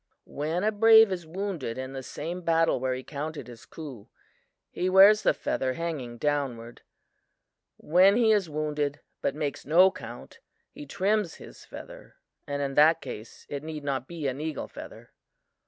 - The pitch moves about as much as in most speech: Yes, average, 4.9 semitones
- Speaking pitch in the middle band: Yes, medium, 155 Hz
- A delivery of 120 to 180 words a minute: Yes, average, 165 wpm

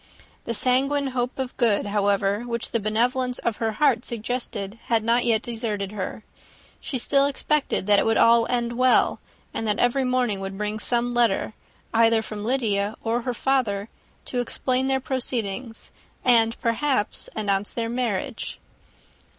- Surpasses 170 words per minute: No, average, 155 wpm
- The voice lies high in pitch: Yes, high, 230 Hz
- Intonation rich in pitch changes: No, average, 2.9 semitones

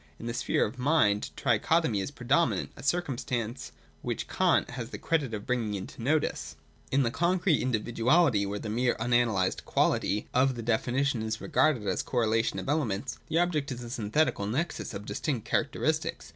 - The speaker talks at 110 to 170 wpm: No, average, 185 wpm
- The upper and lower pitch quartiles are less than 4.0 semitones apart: No, average, 4.8 semitones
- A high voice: No, low, 120 Hz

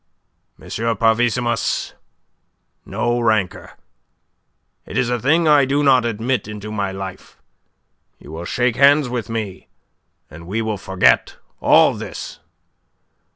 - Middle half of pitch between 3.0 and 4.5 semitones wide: Yes, average, 3.9 semitones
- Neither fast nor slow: No, slow, 120 wpm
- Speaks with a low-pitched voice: Yes, low, 115 Hz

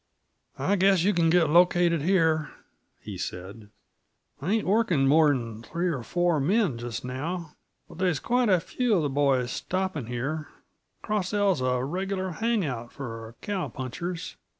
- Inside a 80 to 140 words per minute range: No, average, 160 wpm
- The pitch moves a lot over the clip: Yes, wide, 6.1 semitones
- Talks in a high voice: No, medium, 165 Hz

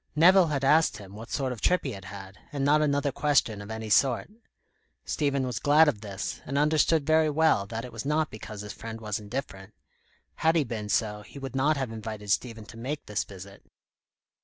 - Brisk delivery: Yes, fast, 210 wpm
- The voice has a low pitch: Yes, low, 125 Hz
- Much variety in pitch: Yes, wide, 5.8 semitones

